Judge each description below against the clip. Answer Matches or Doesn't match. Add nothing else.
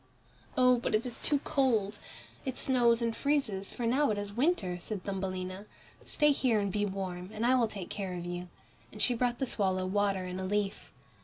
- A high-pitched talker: Matches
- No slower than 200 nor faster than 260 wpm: Matches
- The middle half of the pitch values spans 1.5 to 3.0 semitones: Doesn't match